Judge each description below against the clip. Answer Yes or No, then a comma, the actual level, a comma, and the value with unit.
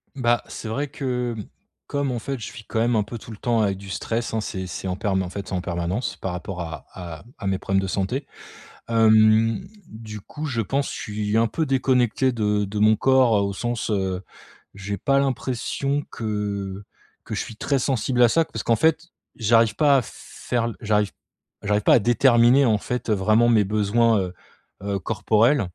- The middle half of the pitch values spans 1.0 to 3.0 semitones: No, average, 3.4 semitones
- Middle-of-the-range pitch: No, low, 110 Hz